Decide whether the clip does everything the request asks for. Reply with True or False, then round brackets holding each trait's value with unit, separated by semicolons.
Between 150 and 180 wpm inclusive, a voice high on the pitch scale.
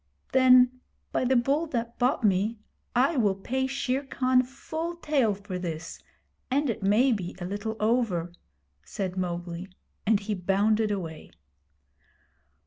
False (135 wpm; 220 Hz)